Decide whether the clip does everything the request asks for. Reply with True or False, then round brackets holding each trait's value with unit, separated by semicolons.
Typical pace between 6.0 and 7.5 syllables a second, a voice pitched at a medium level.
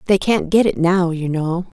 False (4.6 syllables/s; 180 Hz)